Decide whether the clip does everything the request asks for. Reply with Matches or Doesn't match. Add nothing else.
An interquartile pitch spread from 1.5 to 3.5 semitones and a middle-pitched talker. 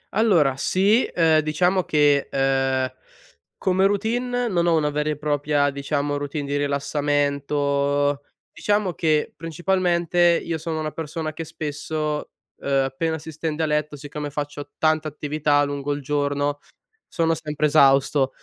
Matches